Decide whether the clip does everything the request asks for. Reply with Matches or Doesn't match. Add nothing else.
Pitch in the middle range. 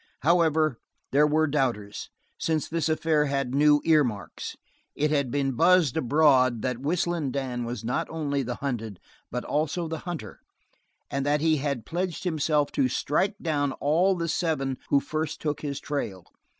Matches